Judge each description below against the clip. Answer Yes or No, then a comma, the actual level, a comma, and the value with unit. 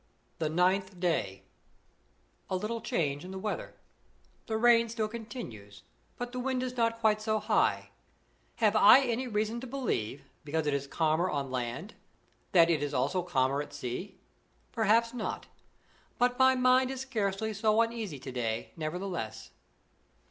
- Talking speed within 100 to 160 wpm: Yes, average, 155 wpm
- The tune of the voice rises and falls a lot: Yes, wide, 8.0 semitones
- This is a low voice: No, high, 195 Hz